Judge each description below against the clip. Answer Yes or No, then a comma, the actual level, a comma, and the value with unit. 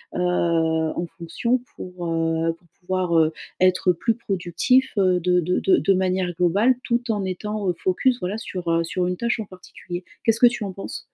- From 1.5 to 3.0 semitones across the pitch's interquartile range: No, average, 3.5 semitones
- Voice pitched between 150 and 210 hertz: Yes, medium, 185 Hz